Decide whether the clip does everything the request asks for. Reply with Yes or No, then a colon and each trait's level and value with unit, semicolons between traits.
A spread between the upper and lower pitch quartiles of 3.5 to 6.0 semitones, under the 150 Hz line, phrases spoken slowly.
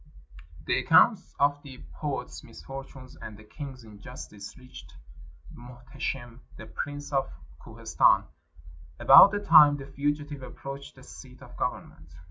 No: average, 2.9 semitones; low, 135 Hz; slow, 125 wpm